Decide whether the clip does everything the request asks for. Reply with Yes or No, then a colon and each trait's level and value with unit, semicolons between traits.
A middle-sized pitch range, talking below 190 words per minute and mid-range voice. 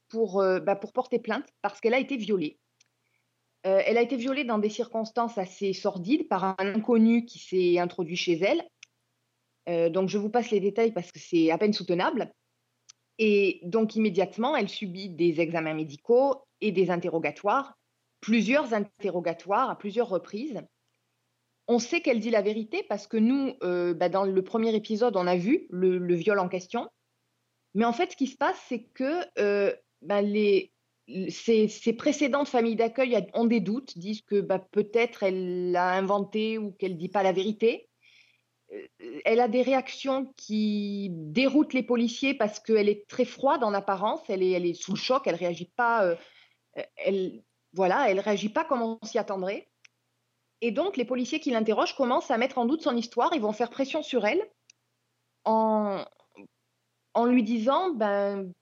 No: average, 4.5 semitones; average, 175 wpm; high, 220 Hz